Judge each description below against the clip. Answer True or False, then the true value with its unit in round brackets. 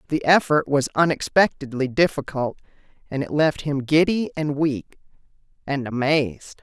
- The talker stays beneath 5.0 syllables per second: True (4.7 syllables/s)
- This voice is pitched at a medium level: True (145 Hz)